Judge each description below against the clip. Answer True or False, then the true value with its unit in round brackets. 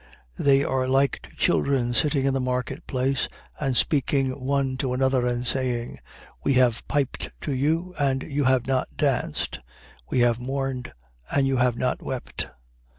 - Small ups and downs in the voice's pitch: True (1.5 semitones)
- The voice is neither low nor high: False (130 Hz)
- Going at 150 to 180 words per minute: True (160 wpm)